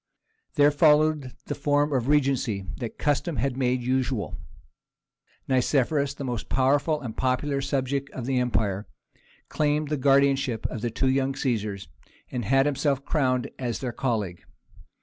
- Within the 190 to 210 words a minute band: No, average, 145 wpm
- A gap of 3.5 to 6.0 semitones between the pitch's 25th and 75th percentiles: No, narrow, 2.6 semitones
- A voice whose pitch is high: No, low, 135 Hz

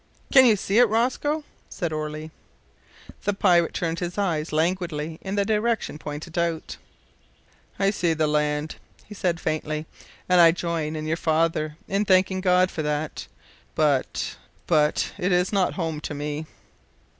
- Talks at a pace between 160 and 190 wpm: No, average, 150 wpm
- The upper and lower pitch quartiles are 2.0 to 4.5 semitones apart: Yes, average, 3.7 semitones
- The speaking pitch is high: No, medium, 170 Hz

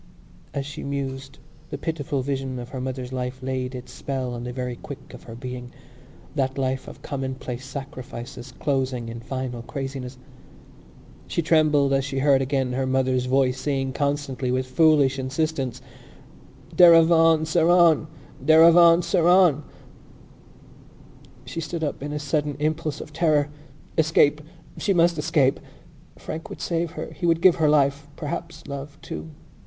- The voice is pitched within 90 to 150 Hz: Yes, medium, 140 Hz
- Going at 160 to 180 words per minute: No, average, 145 wpm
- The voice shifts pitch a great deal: No, average, 3.2 semitones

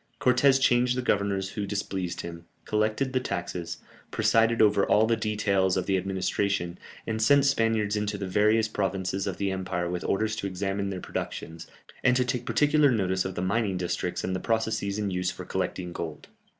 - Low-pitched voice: Yes, low, 100 Hz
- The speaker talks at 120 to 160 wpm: No, average, 185 wpm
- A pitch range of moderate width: Yes, average, 3.1 semitones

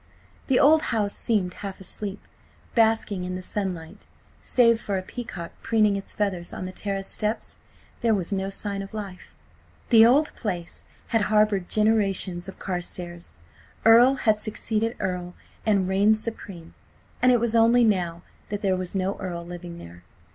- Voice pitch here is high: Yes, high, 200 Hz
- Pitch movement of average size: Yes, average, 3.3 semitones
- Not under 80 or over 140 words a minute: No, average, 160 wpm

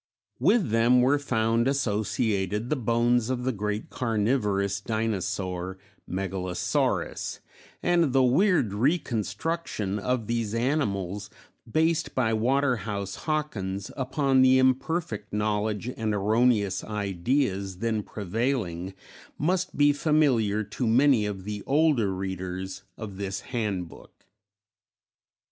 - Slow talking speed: Yes, slow, 105 wpm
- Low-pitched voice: Yes, low, 110 Hz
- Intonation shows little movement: No, average, 4.6 semitones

